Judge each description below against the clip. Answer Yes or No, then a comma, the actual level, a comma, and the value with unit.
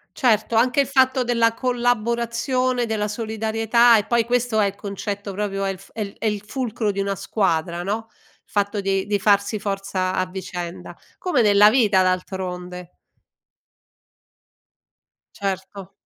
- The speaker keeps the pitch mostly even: No, average, 3.2 semitones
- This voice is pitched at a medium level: No, high, 210 Hz